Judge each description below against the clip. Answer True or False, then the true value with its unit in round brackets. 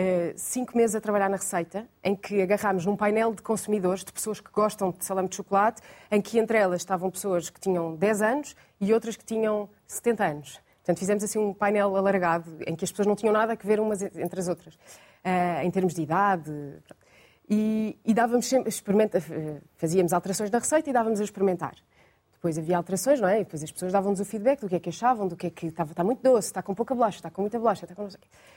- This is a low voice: False (200 Hz)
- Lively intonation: False (3.3 semitones)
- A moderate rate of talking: False (235 wpm)